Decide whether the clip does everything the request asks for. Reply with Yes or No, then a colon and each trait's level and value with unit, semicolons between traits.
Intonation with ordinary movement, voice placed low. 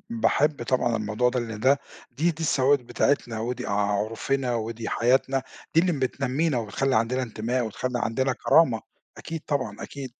Yes: average, 3.3 semitones; low, 125 Hz